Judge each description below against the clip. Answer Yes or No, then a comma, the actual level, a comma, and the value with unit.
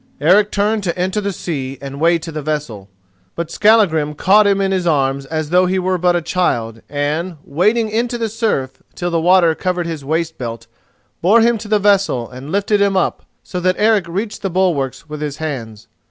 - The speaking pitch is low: No, medium, 175 Hz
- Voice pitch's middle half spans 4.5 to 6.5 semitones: Yes, average, 5.2 semitones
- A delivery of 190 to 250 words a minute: Yes, average, 200 wpm